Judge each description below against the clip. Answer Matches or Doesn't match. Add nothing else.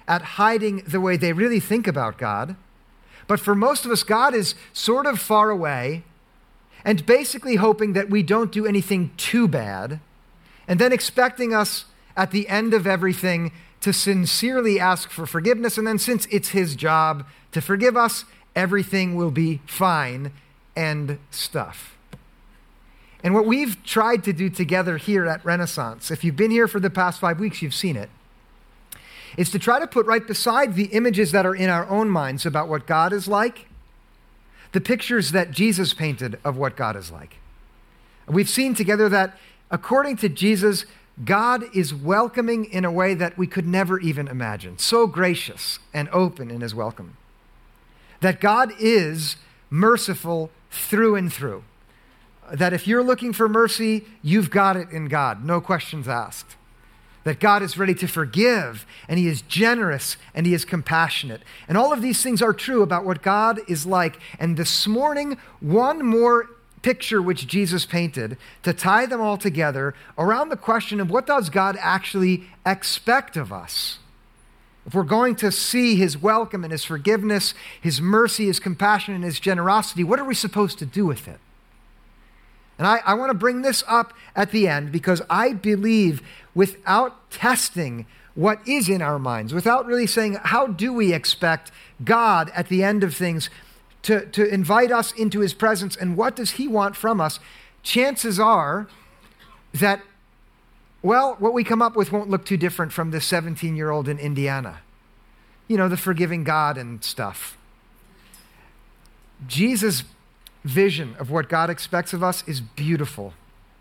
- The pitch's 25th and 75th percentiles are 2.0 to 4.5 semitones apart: Doesn't match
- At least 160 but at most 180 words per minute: Matches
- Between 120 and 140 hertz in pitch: Doesn't match